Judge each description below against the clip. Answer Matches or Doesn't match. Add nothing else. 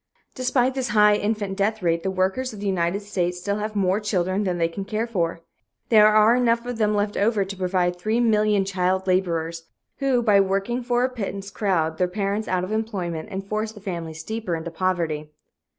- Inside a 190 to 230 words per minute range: Matches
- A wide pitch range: Doesn't match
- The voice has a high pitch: Matches